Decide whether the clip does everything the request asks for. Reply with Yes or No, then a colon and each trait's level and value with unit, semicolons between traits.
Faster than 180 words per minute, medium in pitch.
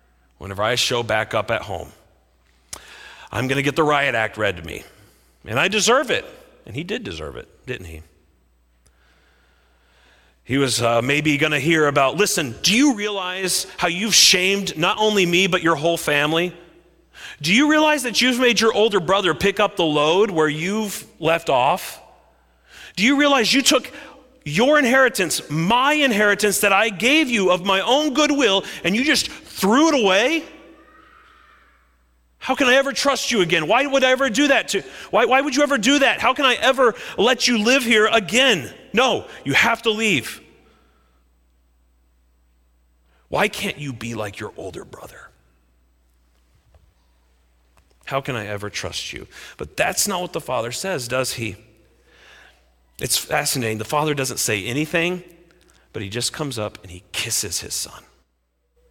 No: average, 165 wpm; medium, 170 Hz